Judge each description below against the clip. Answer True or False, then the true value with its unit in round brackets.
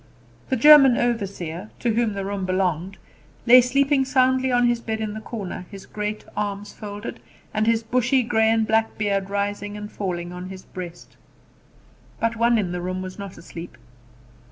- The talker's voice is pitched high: True (210 Hz)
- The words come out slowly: False (175 wpm)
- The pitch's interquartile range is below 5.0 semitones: True (3.6 semitones)